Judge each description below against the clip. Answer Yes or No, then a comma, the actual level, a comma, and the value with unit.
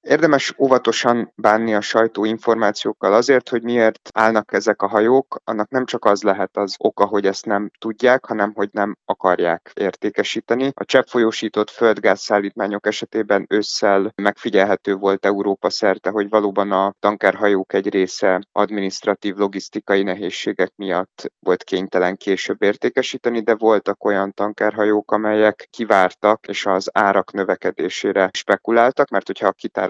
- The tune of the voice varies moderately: No, narrow, 2.2 semitones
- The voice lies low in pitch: Yes, low, 105 Hz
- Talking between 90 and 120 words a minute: No, average, 135 wpm